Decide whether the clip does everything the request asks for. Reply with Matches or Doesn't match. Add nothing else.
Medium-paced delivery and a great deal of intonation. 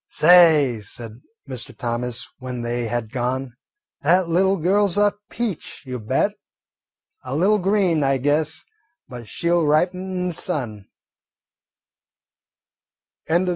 Doesn't match